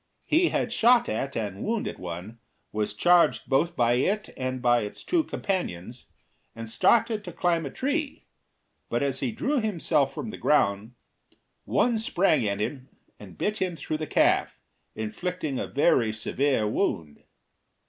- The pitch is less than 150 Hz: Yes, medium, 140 Hz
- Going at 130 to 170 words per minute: Yes, average, 155 wpm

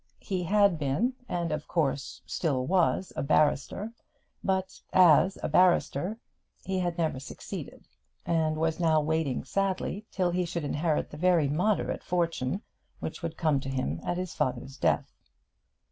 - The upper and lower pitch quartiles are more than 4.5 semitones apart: No, average, 3.8 semitones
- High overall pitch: No, medium, 165 Hz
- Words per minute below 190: Yes, average, 150 wpm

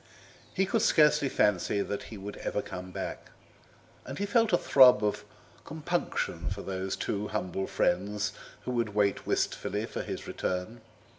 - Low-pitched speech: Yes, low, 105 Hz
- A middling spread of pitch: No, wide, 6.9 semitones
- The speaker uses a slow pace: No, average, 155 wpm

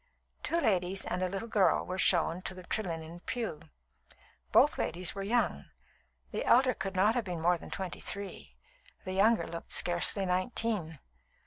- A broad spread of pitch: No, average, 3.2 semitones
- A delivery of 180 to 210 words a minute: No, average, 160 wpm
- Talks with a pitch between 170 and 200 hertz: Yes, medium, 185 Hz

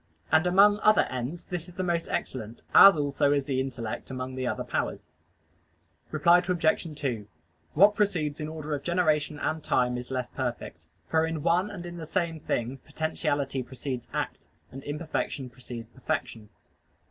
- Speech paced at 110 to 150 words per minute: No, average, 165 wpm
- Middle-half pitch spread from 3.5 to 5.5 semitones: Yes, average, 4.7 semitones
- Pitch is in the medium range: Yes, medium, 150 Hz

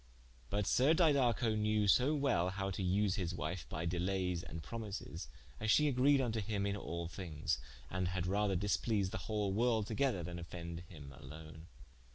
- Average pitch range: Yes, average, 4.3 semitones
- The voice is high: No, very low, 95 Hz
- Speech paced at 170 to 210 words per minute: Yes, average, 175 wpm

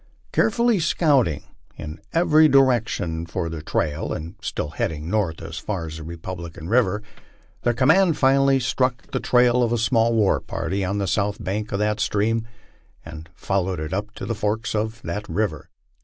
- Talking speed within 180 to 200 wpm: No, average, 170 wpm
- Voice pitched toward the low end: Yes, low, 105 Hz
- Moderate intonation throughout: No, wide, 6.5 semitones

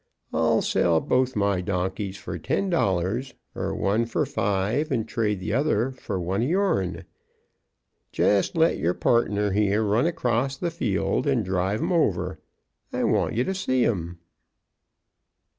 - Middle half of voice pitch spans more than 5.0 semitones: Yes, wide, 5.5 semitones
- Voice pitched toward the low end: Yes, low, 105 Hz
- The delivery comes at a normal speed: Yes, average, 150 wpm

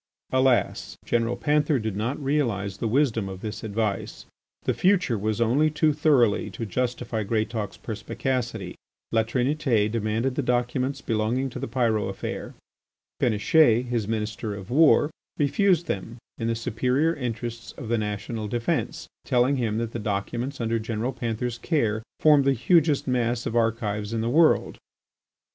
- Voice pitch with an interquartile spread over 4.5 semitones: No, average, 3.4 semitones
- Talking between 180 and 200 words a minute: No, average, 150 wpm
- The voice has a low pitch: Yes, low, 120 Hz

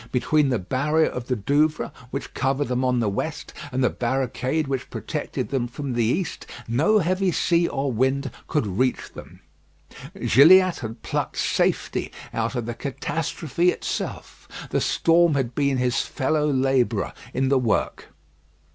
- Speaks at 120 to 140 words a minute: No, average, 155 wpm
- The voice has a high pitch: No, low, 135 Hz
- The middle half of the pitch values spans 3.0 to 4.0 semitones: Yes, average, 3.6 semitones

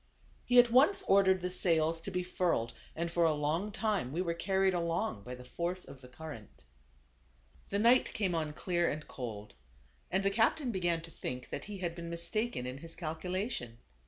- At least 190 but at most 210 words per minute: Yes, average, 195 wpm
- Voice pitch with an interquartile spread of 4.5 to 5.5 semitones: No, average, 4.0 semitones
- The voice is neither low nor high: Yes, medium, 170 Hz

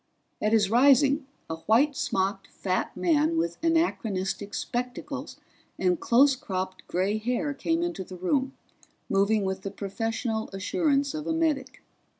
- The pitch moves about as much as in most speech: No, wide, 6.4 semitones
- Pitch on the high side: Yes, high, 220 Hz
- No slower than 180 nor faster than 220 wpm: No, average, 140 wpm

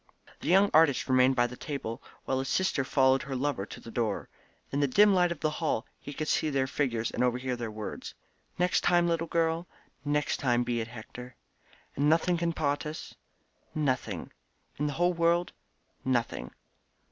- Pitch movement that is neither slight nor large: Yes, average, 4.7 semitones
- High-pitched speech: No, medium, 140 Hz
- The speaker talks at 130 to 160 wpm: No, average, 185 wpm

